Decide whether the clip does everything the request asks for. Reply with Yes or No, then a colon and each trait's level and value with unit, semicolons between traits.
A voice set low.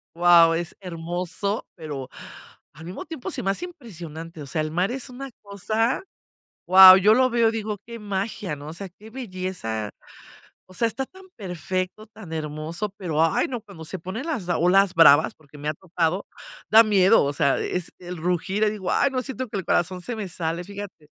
No: medium, 185 Hz